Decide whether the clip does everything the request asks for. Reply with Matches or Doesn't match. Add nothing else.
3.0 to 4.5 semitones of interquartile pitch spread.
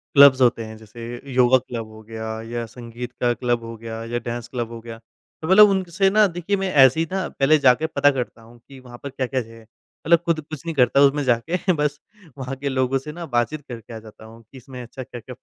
Matches